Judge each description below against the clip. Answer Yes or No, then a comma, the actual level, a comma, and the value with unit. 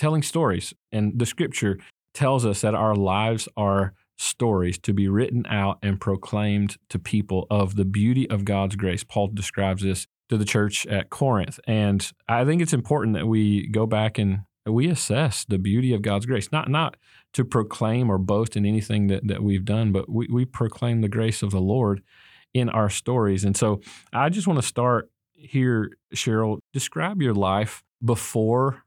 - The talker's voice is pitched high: No, low, 110 Hz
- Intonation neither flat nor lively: Yes, average, 3.4 semitones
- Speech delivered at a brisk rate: No, average, 185 wpm